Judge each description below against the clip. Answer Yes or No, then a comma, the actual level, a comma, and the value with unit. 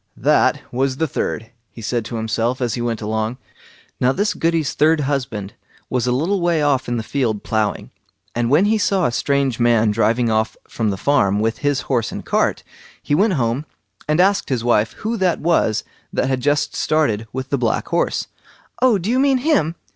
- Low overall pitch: Yes, low, 130 Hz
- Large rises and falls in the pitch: Yes, wide, 5.8 semitones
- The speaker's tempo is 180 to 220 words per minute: Yes, average, 200 wpm